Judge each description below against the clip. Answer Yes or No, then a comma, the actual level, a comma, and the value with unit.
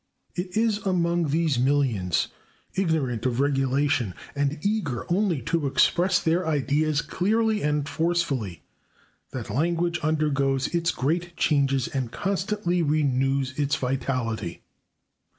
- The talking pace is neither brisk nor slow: No, slow, 115 wpm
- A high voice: No, medium, 150 Hz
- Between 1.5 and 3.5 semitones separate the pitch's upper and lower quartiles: No, average, 4.4 semitones